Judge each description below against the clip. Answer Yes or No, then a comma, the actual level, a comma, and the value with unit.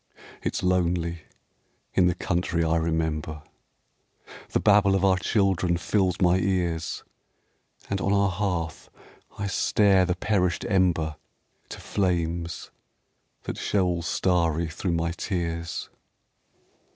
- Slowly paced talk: Yes, slow, 115 wpm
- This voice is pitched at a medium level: No, very low, 90 Hz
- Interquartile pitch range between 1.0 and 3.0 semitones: Yes, narrow, 2.4 semitones